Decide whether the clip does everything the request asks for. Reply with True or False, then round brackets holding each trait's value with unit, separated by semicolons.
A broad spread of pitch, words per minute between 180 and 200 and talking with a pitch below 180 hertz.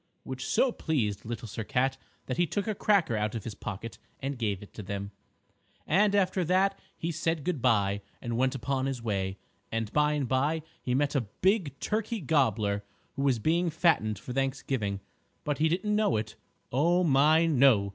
True (6.6 semitones; 190 wpm; 135 Hz)